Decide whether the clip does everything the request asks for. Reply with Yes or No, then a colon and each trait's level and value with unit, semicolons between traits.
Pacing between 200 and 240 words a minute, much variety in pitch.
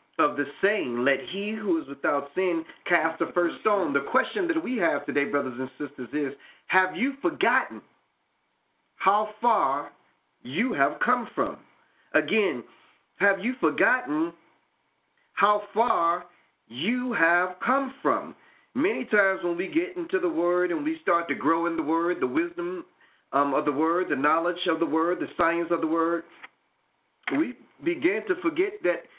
No: average, 160 wpm; wide, 9.0 semitones